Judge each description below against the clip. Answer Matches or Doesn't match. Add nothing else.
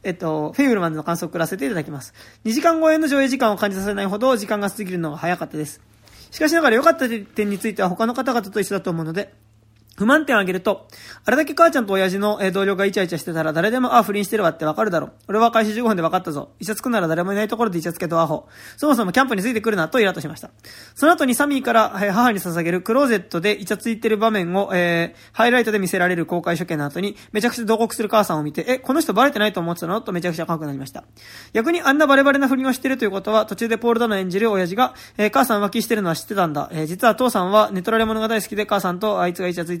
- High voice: Matches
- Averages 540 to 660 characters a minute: Matches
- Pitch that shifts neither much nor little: Matches